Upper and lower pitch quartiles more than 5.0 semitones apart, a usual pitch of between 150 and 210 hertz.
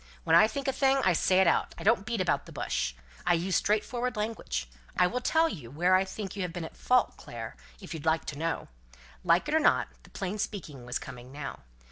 Yes: wide, 5.6 semitones; medium, 185 Hz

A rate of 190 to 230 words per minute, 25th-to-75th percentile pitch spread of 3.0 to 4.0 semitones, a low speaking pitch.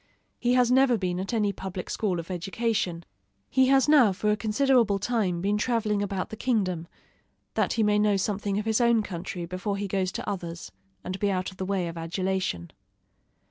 No: average, 195 wpm; average, 3.3 semitones; high, 200 Hz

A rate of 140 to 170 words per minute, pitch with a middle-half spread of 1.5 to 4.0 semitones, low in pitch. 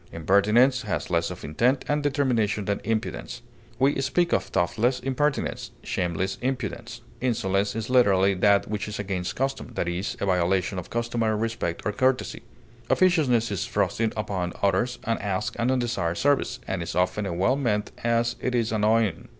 No: average, 160 wpm; average, 4.7 semitones; low, 110 Hz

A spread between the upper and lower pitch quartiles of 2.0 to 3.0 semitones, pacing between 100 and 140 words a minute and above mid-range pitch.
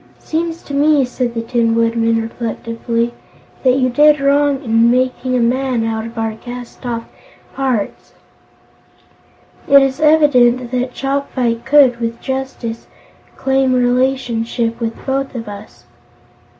Yes: average, 2.7 semitones; slow, 135 wpm; very high, 250 Hz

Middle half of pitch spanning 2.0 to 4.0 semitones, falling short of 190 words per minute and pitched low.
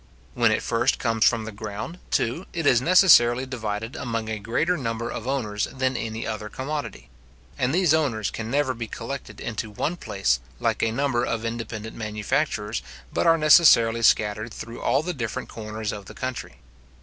Yes: average, 3.5 semitones; average, 175 wpm; low, 115 Hz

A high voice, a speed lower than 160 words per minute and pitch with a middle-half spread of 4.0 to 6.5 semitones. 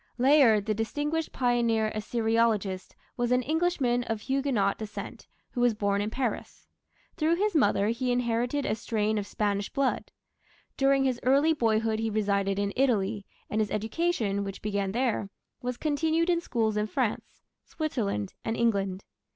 Yes: high, 230 Hz; average, 150 wpm; average, 4.3 semitones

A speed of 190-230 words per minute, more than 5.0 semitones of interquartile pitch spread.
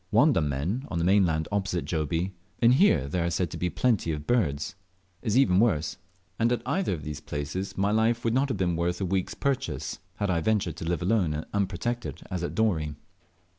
Yes: average, 200 wpm; wide, 5.5 semitones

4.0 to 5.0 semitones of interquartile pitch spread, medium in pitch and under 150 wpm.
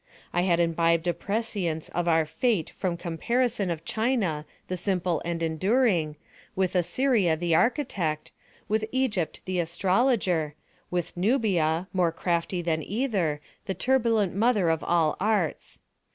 Yes: average, 4.7 semitones; medium, 180 Hz; slow, 135 wpm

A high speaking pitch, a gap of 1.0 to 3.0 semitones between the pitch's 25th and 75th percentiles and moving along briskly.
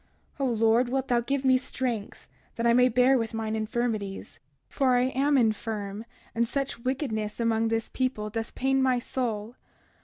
No: high, 235 Hz; average, 2.7 semitones; average, 165 wpm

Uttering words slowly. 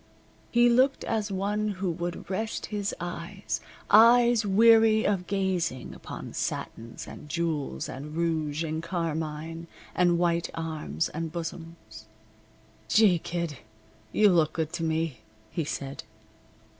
Yes: slow, 125 wpm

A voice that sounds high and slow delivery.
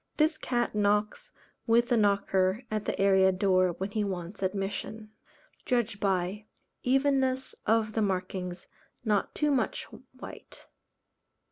Yes: high, 210 Hz; slow, 125 wpm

